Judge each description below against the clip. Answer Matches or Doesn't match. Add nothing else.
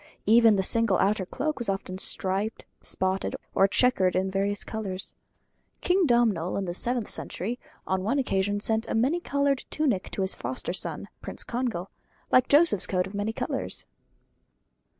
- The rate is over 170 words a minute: Doesn't match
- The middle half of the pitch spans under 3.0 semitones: Doesn't match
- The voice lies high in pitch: Matches